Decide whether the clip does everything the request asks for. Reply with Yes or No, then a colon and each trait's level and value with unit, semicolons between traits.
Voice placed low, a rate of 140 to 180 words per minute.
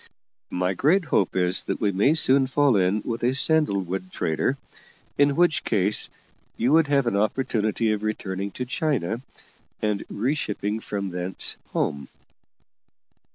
Yes: low, 110 Hz; average, 145 wpm